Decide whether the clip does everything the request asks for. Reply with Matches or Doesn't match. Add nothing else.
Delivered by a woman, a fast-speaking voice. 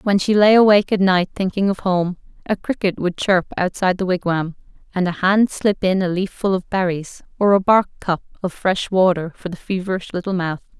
Matches